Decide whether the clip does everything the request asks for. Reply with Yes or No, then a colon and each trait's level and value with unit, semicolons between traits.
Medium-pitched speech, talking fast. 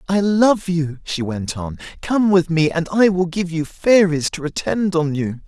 Yes: medium, 170 Hz; fast, 210 wpm